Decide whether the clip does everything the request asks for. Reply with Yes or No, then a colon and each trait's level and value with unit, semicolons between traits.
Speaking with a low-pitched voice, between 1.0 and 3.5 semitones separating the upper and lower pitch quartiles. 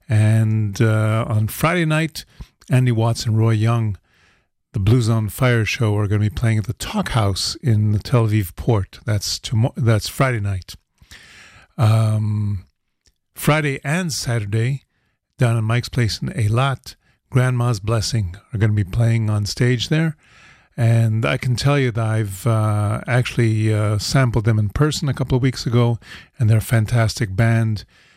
Yes: low, 115 Hz; narrow, 2.5 semitones